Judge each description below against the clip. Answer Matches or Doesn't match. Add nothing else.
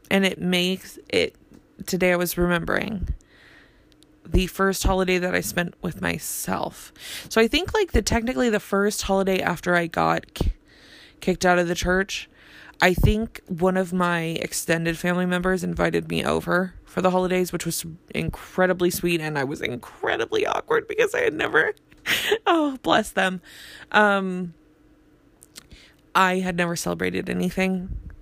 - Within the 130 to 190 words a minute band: Matches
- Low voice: Doesn't match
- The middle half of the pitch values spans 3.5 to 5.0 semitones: Doesn't match